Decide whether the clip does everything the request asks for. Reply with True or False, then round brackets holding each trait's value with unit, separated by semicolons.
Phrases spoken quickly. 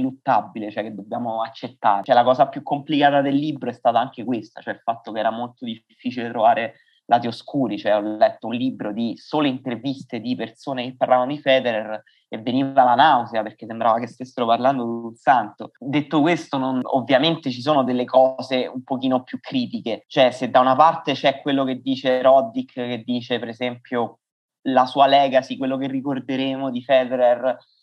True (185 wpm)